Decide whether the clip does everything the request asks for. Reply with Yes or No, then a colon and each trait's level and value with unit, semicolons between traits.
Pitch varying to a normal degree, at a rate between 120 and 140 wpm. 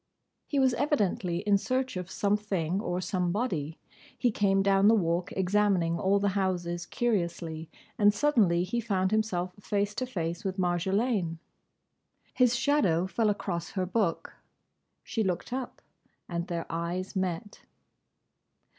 Yes: average, 3.4 semitones; slow, 135 wpm